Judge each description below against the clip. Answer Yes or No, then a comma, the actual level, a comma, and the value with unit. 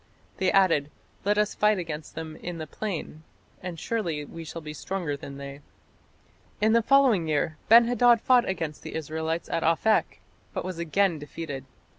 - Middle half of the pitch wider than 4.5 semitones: Yes, average, 5.2 semitones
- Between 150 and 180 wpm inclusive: Yes, average, 170 wpm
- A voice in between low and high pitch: Yes, medium, 165 Hz